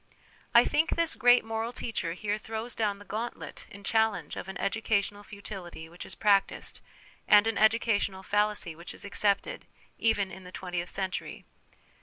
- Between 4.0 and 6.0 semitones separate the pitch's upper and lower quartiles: No, average, 2.7 semitones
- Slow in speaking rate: No, average, 160 wpm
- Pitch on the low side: No, high, 205 Hz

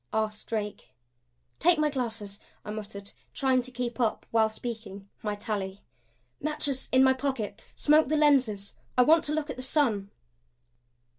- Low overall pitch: No, high, 240 Hz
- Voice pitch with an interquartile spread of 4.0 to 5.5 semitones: Yes, average, 4.7 semitones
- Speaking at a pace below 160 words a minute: Yes, average, 150 wpm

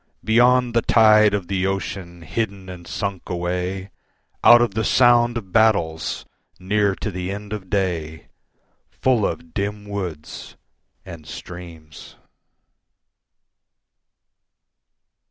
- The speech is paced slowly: Yes, slow, 110 wpm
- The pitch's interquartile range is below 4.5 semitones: Yes, average, 3.5 semitones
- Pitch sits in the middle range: No, very low, 95 Hz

